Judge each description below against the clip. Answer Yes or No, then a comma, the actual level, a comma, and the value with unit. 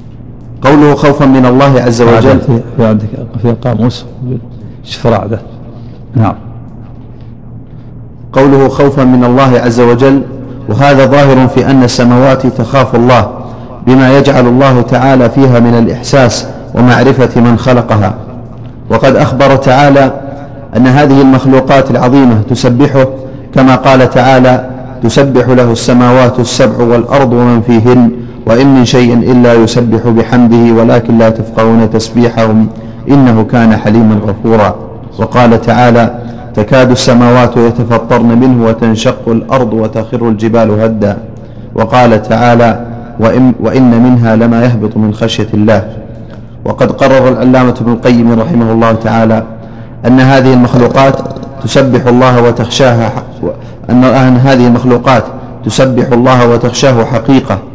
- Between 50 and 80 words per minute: No, average, 105 wpm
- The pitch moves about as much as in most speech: No, narrow, 2.0 semitones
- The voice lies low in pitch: Yes, low, 120 Hz